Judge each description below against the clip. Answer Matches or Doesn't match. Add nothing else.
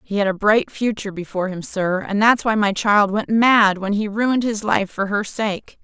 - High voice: Matches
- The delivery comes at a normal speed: Doesn't match